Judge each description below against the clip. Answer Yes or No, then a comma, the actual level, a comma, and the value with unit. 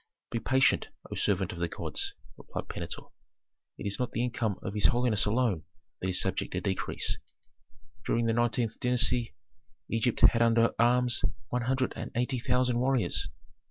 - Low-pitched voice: Yes, low, 120 Hz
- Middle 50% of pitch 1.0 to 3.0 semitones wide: Yes, narrow, 2.4 semitones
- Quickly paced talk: No, average, 160 wpm